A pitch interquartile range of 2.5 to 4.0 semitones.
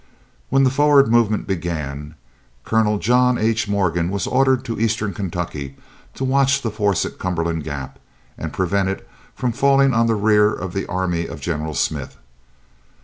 No: wide, 5.5 semitones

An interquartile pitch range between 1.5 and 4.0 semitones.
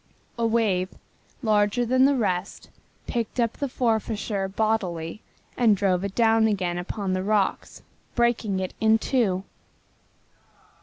Yes: average, 3.5 semitones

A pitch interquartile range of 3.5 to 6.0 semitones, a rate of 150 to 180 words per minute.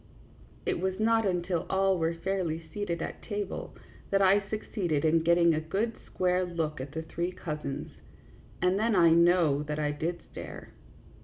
No: average, 3.1 semitones; average, 165 wpm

